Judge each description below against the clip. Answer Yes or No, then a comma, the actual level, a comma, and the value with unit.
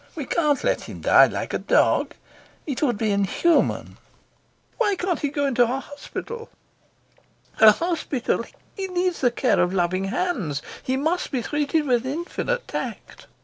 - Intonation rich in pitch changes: Yes, wide, 6.4 semitones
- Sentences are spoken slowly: No, average, 155 wpm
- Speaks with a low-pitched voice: No, very high, 285 Hz